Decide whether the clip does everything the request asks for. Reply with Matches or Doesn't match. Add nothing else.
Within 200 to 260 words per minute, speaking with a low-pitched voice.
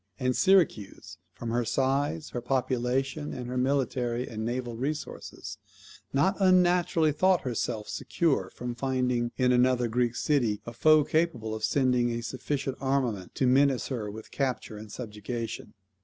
Doesn't match